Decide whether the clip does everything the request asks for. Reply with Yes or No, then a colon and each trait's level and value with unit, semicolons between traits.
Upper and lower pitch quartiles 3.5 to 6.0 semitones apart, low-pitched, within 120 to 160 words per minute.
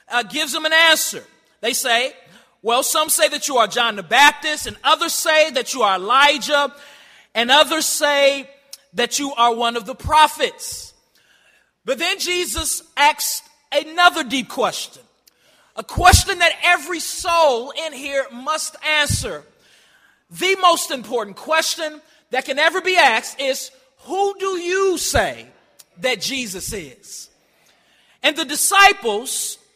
No: average, 4.1 semitones; very high, 300 Hz; average, 140 wpm